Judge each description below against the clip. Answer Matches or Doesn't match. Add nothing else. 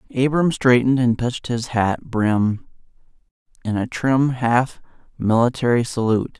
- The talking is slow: Matches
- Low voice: Matches